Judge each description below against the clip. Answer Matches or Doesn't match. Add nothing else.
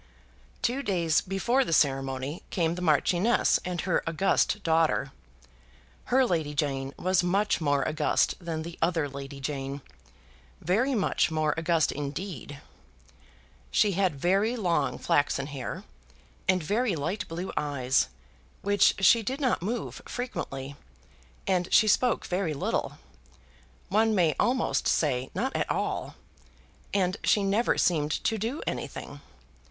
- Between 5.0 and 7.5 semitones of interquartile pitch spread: Matches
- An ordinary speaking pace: Doesn't match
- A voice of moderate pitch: Matches